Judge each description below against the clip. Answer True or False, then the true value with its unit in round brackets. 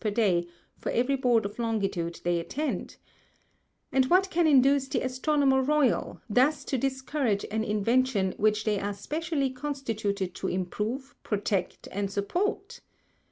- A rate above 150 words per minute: False (140 wpm)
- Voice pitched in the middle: False (240 Hz)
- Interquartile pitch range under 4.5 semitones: False (5.2 semitones)